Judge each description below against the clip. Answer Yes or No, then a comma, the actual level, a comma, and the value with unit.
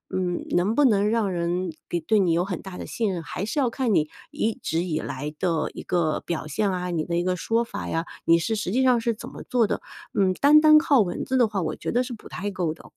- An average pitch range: Yes, average, 4.9 semitones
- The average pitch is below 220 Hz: Yes, high, 190 Hz